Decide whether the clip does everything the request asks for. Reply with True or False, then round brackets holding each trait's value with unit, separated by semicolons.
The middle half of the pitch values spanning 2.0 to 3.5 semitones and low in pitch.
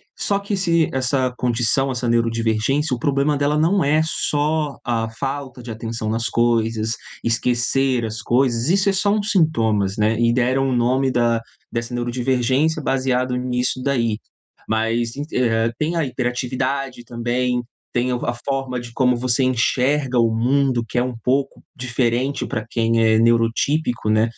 True (2.7 semitones; 125 Hz)